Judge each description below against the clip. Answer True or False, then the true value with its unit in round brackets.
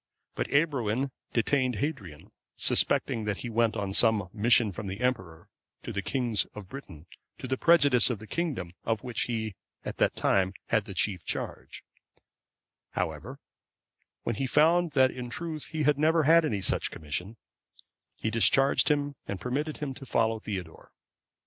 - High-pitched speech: False (120 Hz)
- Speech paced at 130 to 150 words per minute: False (160 wpm)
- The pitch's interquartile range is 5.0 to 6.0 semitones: True (5.6 semitones)